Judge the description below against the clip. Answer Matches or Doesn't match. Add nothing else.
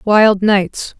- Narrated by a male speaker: Doesn't match